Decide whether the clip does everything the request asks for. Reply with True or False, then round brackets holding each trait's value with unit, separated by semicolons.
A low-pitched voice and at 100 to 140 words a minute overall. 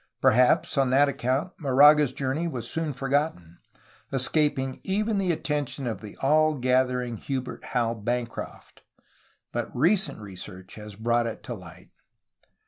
True (130 Hz; 135 wpm)